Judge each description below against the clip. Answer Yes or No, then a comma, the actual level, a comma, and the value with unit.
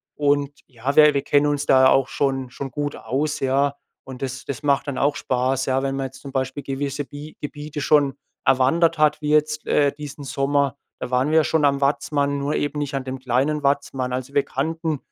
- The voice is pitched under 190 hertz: Yes, medium, 140 Hz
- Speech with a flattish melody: Yes, narrow, 1.7 semitones